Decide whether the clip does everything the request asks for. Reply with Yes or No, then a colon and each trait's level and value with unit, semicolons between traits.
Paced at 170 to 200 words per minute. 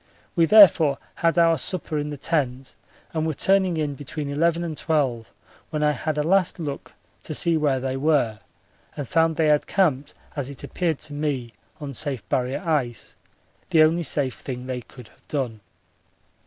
Yes: average, 180 wpm